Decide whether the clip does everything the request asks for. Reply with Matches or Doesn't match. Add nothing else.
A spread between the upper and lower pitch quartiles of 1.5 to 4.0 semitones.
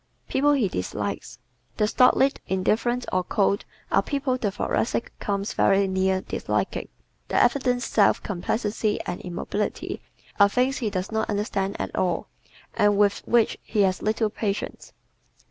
Matches